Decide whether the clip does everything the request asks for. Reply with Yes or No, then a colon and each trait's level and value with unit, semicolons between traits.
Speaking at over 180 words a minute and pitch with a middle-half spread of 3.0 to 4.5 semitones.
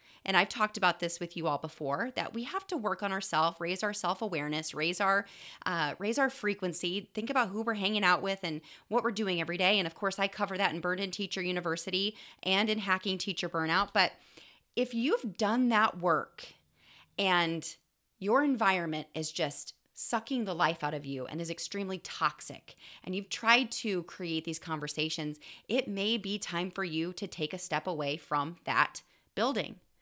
Yes: average, 190 wpm; average, 4.1 semitones